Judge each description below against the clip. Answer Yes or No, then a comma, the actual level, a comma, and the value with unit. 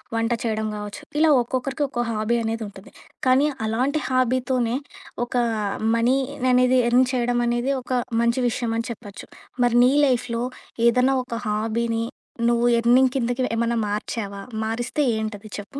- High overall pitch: Yes, high, 240 Hz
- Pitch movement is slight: Yes, narrow, 2.0 semitones